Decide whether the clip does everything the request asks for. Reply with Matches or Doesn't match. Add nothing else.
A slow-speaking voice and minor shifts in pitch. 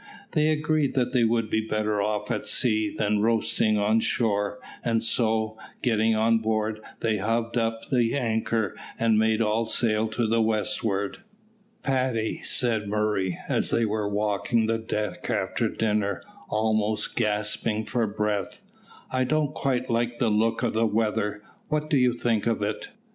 Doesn't match